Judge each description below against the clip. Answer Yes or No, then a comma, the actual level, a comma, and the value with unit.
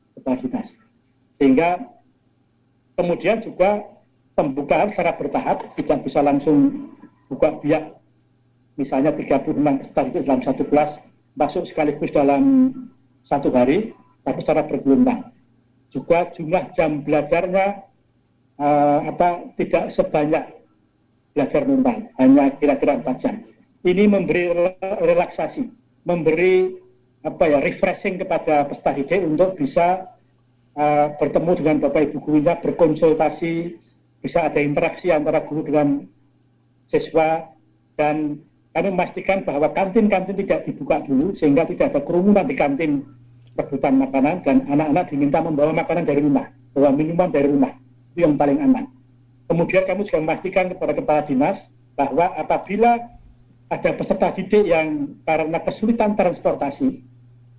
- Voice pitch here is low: No, medium, 155 Hz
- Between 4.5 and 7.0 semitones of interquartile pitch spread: Yes, average, 5.1 semitones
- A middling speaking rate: Yes, average, 115 wpm